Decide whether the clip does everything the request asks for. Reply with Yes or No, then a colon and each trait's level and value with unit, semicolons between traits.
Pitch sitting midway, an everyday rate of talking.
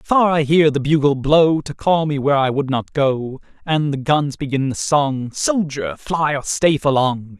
No: medium, 145 Hz; fast, 210 wpm